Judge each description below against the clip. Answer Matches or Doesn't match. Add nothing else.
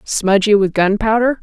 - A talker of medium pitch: Doesn't match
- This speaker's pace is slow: Matches